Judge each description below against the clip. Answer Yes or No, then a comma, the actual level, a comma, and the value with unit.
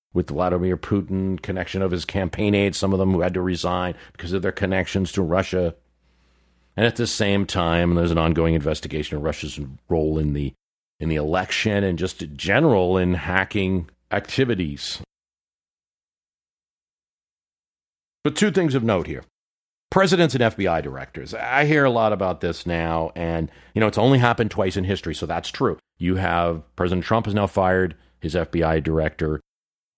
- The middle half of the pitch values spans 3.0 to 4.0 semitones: Yes, average, 3.4 semitones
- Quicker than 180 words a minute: No, average, 170 wpm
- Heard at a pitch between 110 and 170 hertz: No, very low, 90 Hz